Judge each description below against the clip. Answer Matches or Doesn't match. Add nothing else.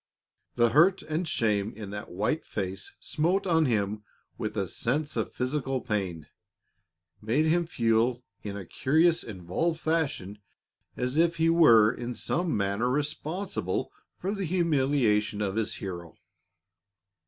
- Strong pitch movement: Matches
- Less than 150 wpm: Matches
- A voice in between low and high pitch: Doesn't match